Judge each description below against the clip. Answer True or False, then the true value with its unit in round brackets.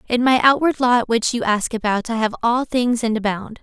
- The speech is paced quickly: True (230 wpm)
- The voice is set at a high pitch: True (235 Hz)